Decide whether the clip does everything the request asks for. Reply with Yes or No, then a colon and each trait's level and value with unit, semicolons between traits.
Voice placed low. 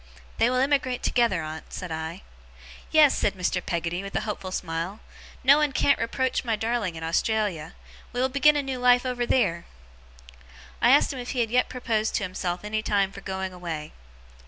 No: high, 215 Hz